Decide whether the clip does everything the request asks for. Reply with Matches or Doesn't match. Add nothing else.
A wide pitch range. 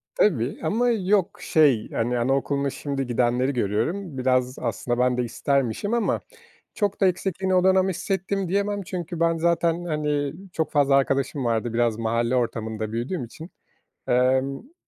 Matches